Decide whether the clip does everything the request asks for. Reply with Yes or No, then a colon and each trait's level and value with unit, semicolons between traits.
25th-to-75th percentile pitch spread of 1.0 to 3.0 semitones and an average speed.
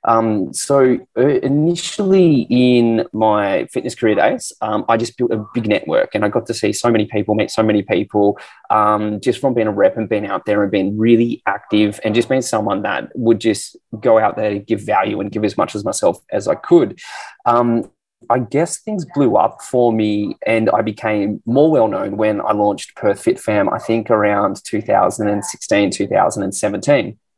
Yes: narrow, 2.5 semitones; average, 195 wpm